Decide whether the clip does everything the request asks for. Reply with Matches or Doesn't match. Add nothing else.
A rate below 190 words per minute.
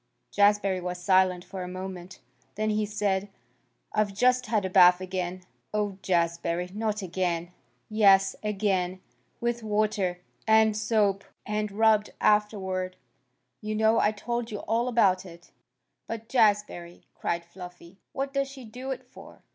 Matches